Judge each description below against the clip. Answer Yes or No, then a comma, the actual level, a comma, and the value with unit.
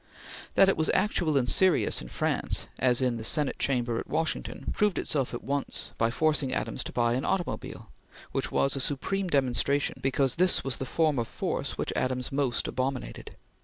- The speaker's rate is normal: Yes, average, 185 wpm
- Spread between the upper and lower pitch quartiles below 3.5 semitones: No, average, 3.9 semitones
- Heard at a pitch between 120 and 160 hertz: Yes, low, 135 Hz